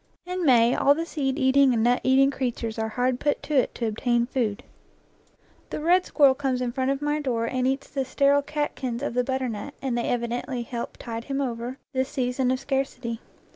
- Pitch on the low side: No, very high, 260 Hz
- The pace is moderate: No, fast, 210 wpm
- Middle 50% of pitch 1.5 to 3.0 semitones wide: Yes, narrow, 2.6 semitones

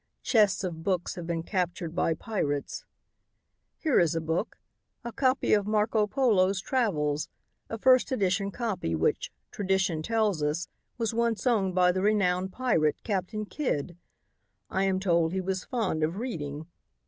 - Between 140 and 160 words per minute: Yes, average, 150 wpm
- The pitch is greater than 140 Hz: Yes, high, 190 Hz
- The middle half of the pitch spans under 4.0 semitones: No, average, 4.7 semitones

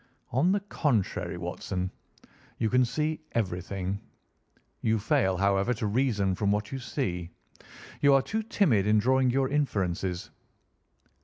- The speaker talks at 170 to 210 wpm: No, slow, 135 wpm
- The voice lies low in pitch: Yes, low, 110 Hz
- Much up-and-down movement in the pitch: Yes, wide, 5.7 semitones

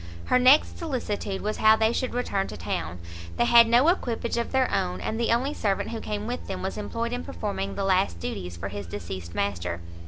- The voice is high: Yes, high, 205 Hz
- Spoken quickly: Yes, fast, 215 wpm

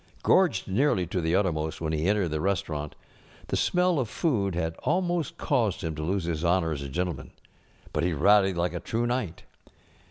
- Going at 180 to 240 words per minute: Yes, average, 190 wpm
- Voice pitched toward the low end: Yes, very low, 90 Hz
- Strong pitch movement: Yes, wide, 5.8 semitones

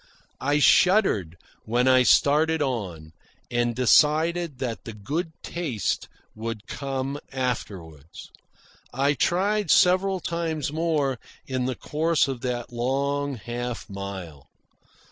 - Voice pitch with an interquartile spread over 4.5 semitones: Yes, average, 5.2 semitones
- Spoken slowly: Yes, slow, 110 wpm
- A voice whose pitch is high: No, low, 130 Hz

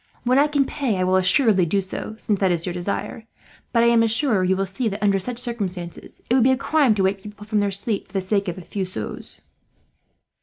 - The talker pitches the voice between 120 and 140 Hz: No, high, 205 Hz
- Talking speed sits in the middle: No, fast, 250 wpm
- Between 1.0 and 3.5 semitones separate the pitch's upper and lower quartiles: No, average, 4.0 semitones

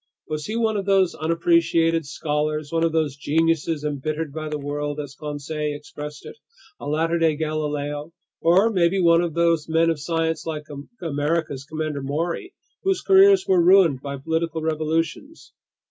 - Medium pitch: Yes, medium, 160 Hz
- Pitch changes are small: Yes, narrow, 2.1 semitones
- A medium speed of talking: Yes, average, 160 wpm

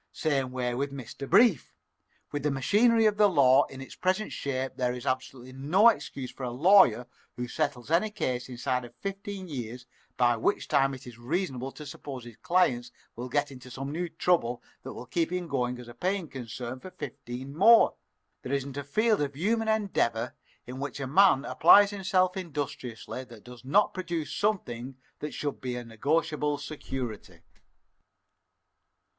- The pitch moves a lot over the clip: Yes, wide, 6.2 semitones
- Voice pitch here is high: No, medium, 140 Hz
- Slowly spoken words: No, average, 175 wpm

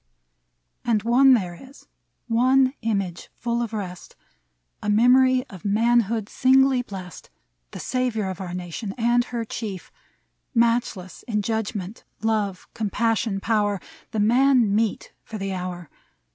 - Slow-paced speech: Yes, slow, 130 wpm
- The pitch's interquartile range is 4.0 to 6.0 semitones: No, average, 3.5 semitones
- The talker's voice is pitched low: No, high, 220 Hz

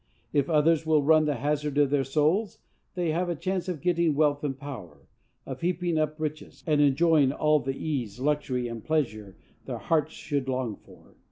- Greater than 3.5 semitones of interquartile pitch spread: No, average, 2.8 semitones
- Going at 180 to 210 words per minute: Yes, average, 185 wpm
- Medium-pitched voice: Yes, medium, 150 Hz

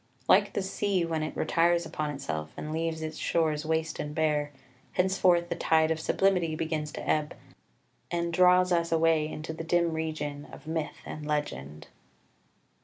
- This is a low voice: No, medium, 160 Hz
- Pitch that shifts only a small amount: Yes, narrow, 2.0 semitones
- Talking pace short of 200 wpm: Yes, average, 165 wpm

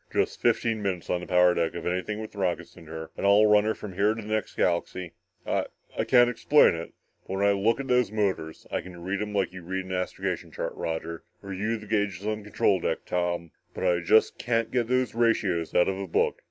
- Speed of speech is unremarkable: No, fast, 240 wpm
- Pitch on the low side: Yes, low, 100 Hz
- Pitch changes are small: No, average, 3.4 semitones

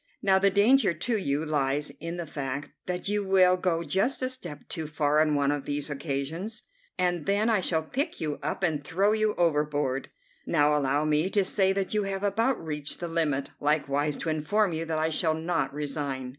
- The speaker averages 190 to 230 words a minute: Yes, average, 200 wpm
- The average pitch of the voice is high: No, medium, 160 Hz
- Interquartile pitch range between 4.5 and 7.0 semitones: Yes, average, 4.8 semitones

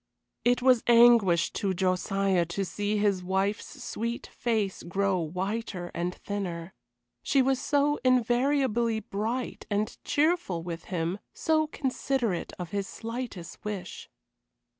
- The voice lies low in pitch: No, high, 205 Hz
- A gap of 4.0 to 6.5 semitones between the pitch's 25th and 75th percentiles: Yes, average, 4.9 semitones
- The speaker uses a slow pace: Yes, slow, 120 wpm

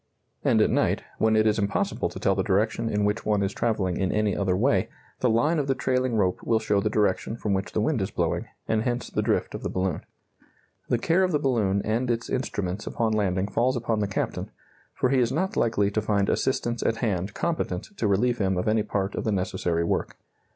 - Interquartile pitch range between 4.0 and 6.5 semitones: No, average, 3.4 semitones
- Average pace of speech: No, fast, 230 wpm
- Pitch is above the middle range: No, low, 110 Hz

